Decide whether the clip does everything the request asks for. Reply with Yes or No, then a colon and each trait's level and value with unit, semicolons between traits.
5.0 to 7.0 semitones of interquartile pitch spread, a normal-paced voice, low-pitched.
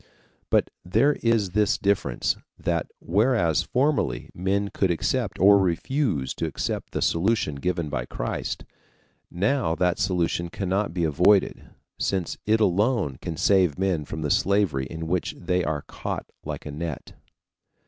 No: average, 3.9 semitones; average, 145 wpm; very low, 90 Hz